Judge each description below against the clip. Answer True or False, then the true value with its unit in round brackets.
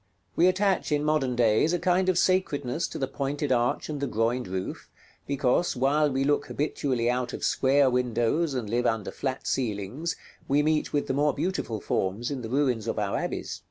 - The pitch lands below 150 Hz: True (135 Hz)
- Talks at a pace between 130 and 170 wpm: False (195 wpm)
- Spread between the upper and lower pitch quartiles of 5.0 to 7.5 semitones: False (3.9 semitones)